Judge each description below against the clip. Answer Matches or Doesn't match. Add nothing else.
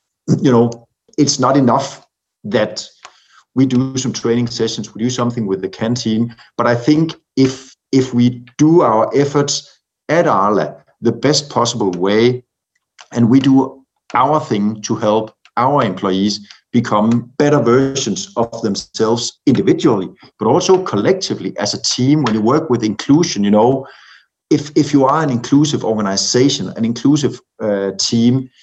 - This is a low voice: Matches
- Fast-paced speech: Doesn't match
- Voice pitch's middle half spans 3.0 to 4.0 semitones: Matches